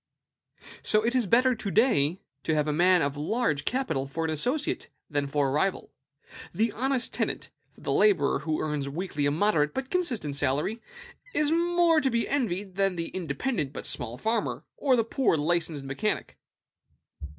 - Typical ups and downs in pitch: No, wide, 8.8 semitones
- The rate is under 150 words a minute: No, average, 170 wpm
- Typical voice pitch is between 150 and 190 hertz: Yes, medium, 185 Hz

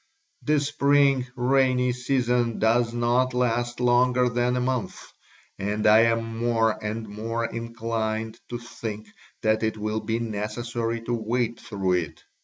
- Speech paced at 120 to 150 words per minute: Yes, average, 140 wpm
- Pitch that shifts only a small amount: Yes, narrow, 1.9 semitones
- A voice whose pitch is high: No, low, 115 Hz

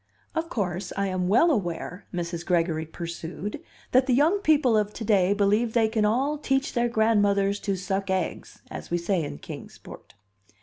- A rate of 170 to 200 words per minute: Yes, average, 180 wpm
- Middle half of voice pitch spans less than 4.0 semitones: No, average, 4.9 semitones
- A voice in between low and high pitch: No, high, 205 Hz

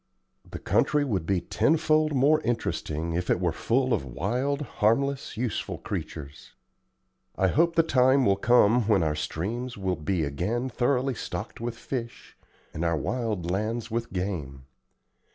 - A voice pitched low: Yes, low, 115 Hz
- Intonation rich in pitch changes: Yes, wide, 6.4 semitones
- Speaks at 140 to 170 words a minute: Yes, average, 150 wpm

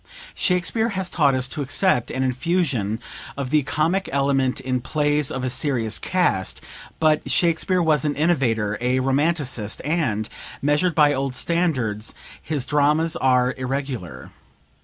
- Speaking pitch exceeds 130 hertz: Yes, medium, 140 Hz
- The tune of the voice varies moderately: Yes, average, 4.0 semitones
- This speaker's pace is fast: No, average, 140 wpm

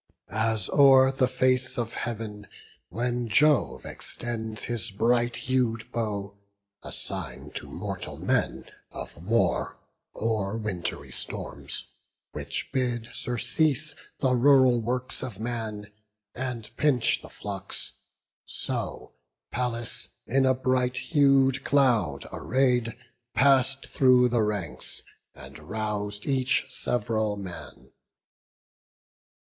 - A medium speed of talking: No, slow, 105 wpm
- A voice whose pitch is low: Yes, low, 120 Hz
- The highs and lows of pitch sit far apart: No, average, 3.1 semitones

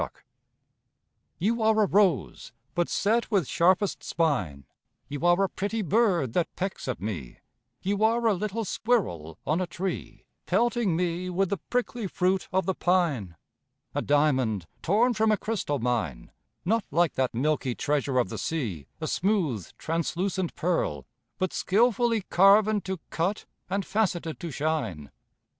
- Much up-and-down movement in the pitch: Yes, wide, 6.3 semitones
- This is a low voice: No, medium, 180 Hz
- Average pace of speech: Yes, average, 150 wpm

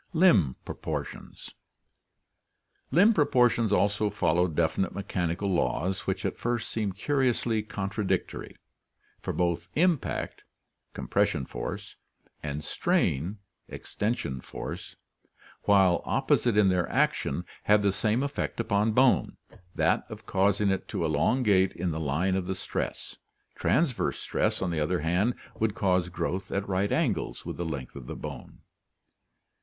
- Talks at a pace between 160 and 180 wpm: No, slow, 135 wpm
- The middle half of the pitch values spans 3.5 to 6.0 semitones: Yes, average, 4.3 semitones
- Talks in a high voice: No, low, 100 Hz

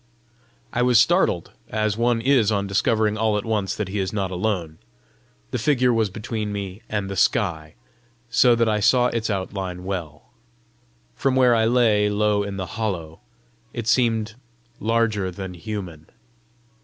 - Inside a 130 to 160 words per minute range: Yes, average, 155 wpm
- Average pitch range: Yes, average, 3.1 semitones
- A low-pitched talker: Yes, low, 105 Hz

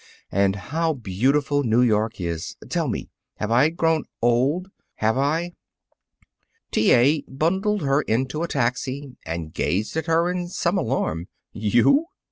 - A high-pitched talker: No, low, 135 Hz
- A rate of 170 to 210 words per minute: No, average, 140 wpm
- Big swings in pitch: Yes, wide, 6.8 semitones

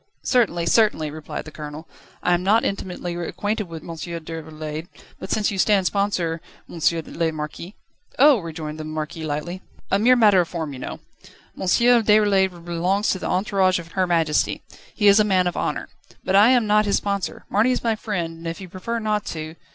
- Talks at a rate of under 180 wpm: No, average, 195 wpm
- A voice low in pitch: No, medium, 180 Hz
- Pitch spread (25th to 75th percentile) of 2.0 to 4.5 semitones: Yes, average, 4.2 semitones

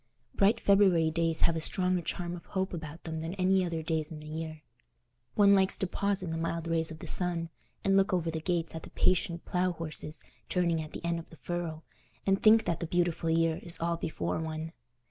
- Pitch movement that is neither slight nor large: No, narrow, 2.2 semitones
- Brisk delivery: Yes, fast, 220 wpm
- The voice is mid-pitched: Yes, medium, 170 Hz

